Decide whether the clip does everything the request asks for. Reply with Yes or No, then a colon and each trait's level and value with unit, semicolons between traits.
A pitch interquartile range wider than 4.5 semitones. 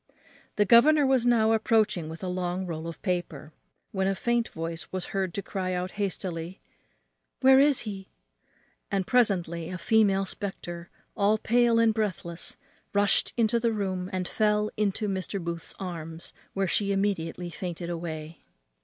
No: average, 3.7 semitones